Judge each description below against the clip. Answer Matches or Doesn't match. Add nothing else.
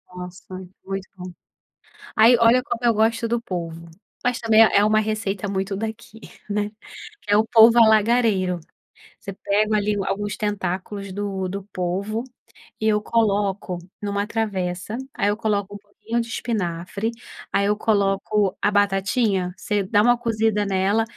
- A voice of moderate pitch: Doesn't match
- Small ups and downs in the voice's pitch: Matches